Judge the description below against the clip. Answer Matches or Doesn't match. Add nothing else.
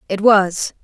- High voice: Matches